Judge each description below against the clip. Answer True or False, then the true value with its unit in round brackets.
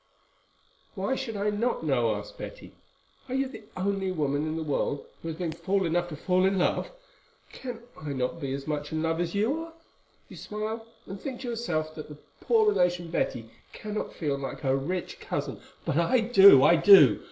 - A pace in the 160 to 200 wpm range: True (195 wpm)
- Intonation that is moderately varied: False (5.9 semitones)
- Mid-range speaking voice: True (175 Hz)